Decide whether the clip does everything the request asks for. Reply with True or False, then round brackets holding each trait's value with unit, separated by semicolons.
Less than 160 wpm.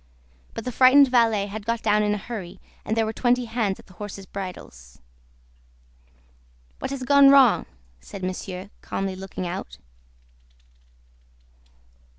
True (140 wpm)